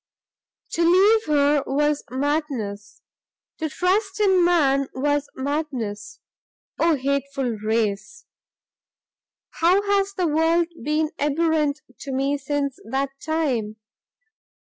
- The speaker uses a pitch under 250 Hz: No, very high, 290 Hz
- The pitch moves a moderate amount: Yes, average, 3.8 semitones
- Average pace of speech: No, slow, 100 wpm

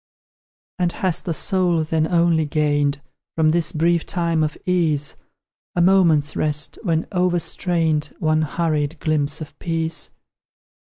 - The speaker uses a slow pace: Yes, slow, 125 wpm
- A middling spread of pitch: No, narrow, 2.1 semitones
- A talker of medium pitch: Yes, medium, 160 Hz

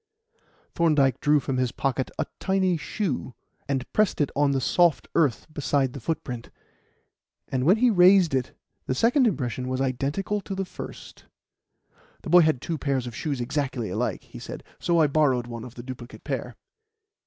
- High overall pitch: No, medium, 140 Hz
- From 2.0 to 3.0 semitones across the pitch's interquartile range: No, average, 5.0 semitones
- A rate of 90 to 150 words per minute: No, average, 175 wpm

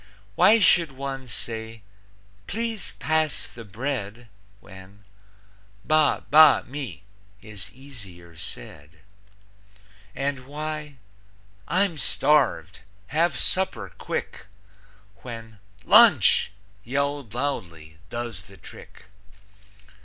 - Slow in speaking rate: Yes, slow, 85 wpm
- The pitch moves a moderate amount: No, wide, 6.5 semitones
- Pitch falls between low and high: No, low, 130 Hz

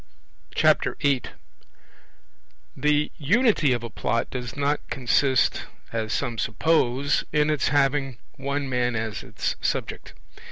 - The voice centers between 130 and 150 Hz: Yes, low, 135 Hz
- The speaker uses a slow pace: Yes, slow, 115 wpm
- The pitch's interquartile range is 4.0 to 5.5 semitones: No, average, 3.2 semitones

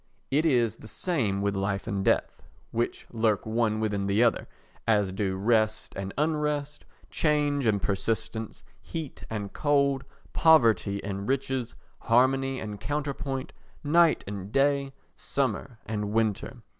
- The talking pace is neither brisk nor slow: No, slow, 130 wpm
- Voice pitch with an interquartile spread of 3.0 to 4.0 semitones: No, average, 5.2 semitones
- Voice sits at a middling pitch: No, low, 115 Hz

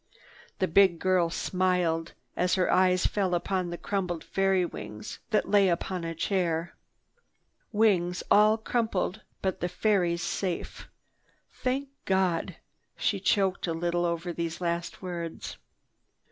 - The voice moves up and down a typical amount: No, narrow, 2.2 semitones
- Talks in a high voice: No, medium, 180 Hz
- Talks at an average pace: No, slow, 130 wpm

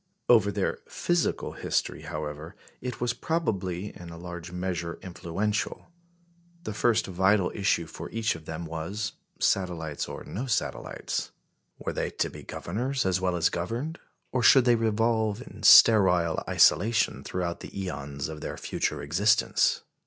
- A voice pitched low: Yes, very low, 95 Hz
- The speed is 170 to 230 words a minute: No, average, 145 wpm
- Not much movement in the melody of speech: No, average, 4.8 semitones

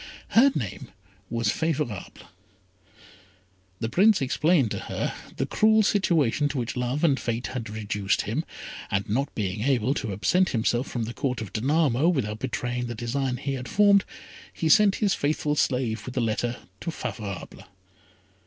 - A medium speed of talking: Yes, average, 160 wpm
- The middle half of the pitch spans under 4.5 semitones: No, wide, 5.4 semitones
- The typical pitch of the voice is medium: No, low, 125 Hz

